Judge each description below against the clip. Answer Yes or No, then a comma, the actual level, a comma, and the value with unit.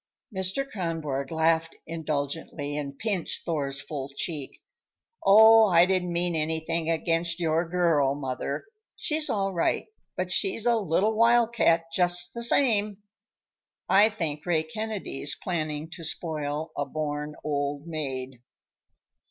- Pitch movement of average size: Yes, average, 4.3 semitones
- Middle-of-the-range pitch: Yes, medium, 165 Hz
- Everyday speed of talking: No, slow, 125 wpm